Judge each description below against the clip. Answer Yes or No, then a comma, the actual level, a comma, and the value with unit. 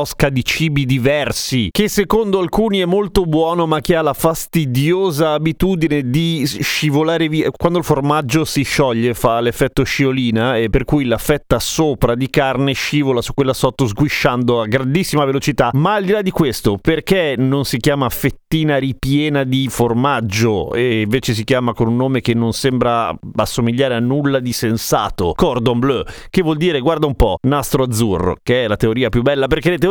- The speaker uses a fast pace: Yes, fast, 180 wpm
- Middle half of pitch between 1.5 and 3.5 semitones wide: No, average, 4.3 semitones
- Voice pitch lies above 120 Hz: Yes, medium, 140 Hz